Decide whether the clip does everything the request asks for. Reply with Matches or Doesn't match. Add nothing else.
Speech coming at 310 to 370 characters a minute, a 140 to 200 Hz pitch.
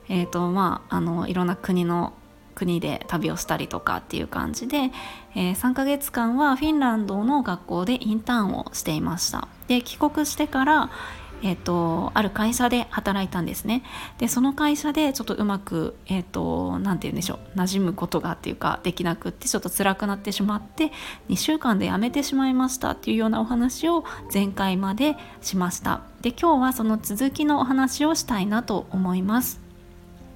Doesn't match